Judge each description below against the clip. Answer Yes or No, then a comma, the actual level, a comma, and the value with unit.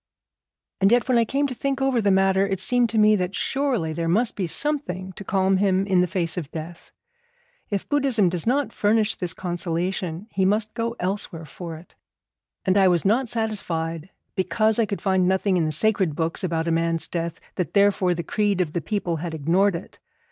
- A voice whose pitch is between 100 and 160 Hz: No, high, 190 Hz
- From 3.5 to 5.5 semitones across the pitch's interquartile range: Yes, average, 4.0 semitones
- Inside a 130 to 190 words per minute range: No, fast, 205 wpm